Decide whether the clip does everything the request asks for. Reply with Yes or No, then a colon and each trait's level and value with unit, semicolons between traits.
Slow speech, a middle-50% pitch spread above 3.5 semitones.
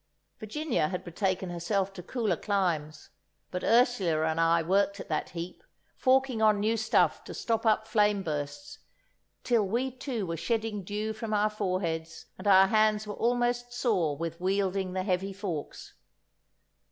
No: average, 155 wpm; average, 3.9 semitones